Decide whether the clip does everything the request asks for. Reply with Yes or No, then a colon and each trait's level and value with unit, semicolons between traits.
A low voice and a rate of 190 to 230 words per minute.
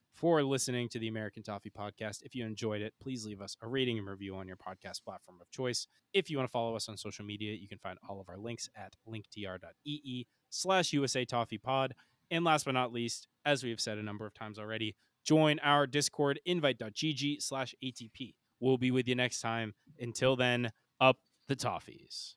Yes: low, 120 Hz; fast, 205 wpm